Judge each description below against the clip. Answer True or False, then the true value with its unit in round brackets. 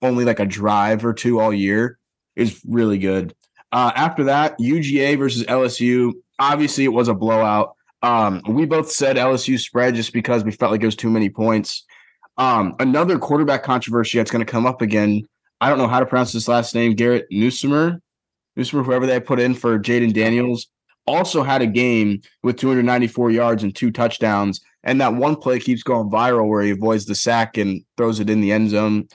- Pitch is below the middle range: True (120 Hz)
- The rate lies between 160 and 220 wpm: True (195 wpm)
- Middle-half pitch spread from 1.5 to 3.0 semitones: True (2.5 semitones)